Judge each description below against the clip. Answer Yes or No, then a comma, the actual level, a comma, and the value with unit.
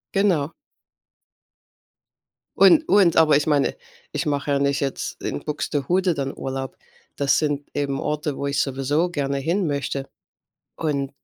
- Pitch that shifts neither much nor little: No, narrow, 2.3 semitones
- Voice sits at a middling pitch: Yes, medium, 145 Hz